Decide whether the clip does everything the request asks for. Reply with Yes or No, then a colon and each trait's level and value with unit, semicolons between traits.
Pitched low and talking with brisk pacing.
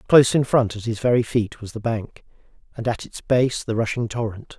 Yes: low, 115 Hz; fast, 220 wpm